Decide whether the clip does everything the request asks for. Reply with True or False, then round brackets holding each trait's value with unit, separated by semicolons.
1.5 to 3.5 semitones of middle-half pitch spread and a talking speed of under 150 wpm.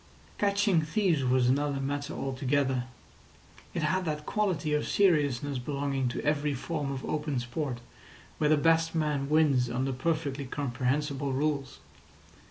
True (2.6 semitones; 135 wpm)